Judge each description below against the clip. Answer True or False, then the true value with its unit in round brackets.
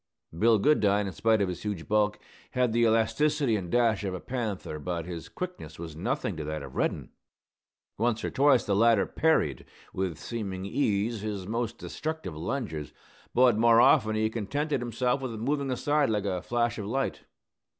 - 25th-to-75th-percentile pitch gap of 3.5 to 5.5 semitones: True (4.3 semitones)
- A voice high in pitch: False (110 Hz)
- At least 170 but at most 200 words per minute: True (175 wpm)